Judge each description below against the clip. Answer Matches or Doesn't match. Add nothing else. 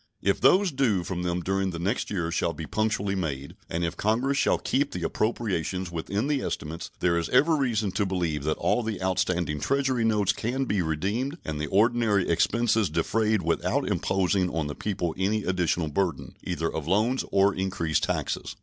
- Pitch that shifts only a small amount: Doesn't match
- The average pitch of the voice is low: Matches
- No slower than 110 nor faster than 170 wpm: Doesn't match